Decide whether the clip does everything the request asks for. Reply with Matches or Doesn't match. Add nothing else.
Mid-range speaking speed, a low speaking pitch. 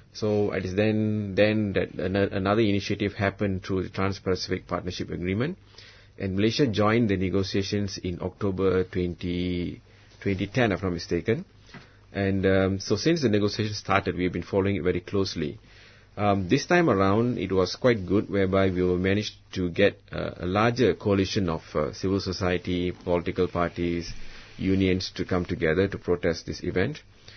Matches